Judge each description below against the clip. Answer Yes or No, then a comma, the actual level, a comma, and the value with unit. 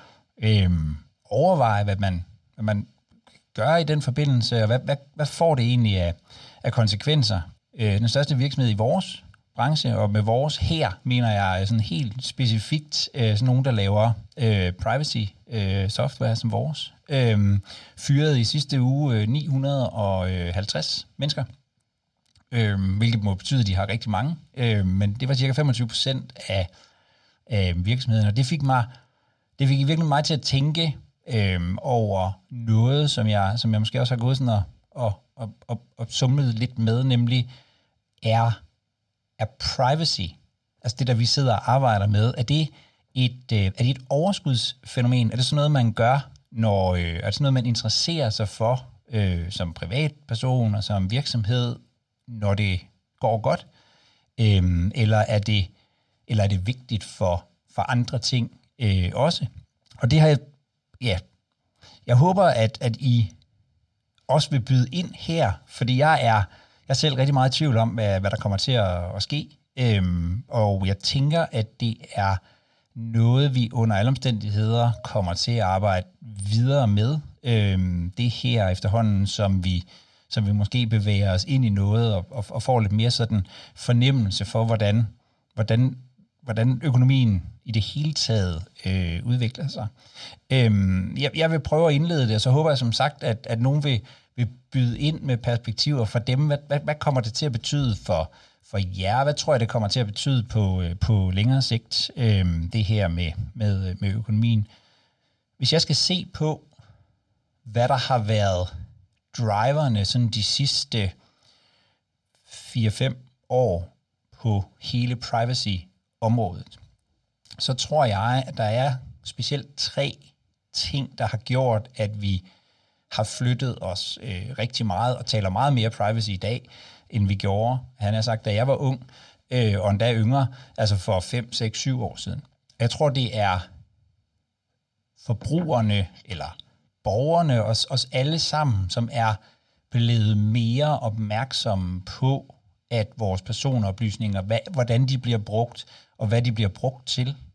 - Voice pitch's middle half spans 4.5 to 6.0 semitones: No, average, 3.9 semitones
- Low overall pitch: Yes, low, 115 Hz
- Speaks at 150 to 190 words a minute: Yes, average, 160 wpm